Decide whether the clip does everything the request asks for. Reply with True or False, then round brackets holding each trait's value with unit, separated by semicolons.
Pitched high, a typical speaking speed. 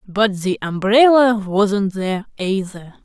False (205 Hz; 120 wpm)